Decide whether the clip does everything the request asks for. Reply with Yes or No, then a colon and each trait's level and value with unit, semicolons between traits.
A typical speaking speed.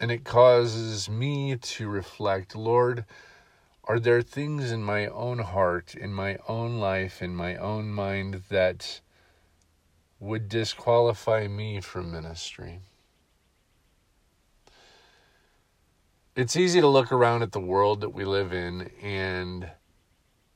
No: slow, 120 wpm